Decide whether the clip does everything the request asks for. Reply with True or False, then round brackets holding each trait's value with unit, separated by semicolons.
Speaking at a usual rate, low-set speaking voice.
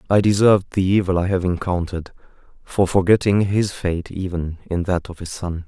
True (180 wpm; 90 Hz)